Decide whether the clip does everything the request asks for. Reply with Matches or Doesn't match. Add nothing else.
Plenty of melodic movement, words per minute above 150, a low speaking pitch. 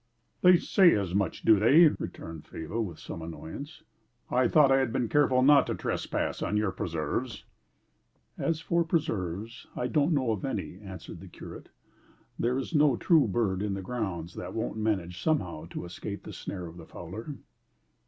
Matches